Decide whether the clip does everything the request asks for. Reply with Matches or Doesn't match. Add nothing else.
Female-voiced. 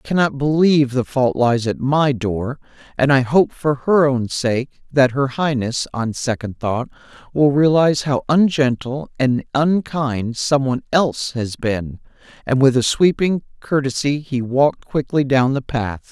Doesn't match